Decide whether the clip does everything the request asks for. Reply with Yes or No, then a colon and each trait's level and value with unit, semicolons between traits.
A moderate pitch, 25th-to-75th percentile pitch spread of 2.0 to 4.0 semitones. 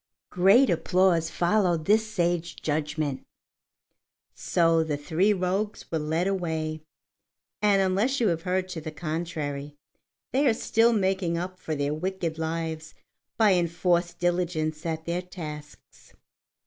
Yes: medium, 170 Hz; average, 3.0 semitones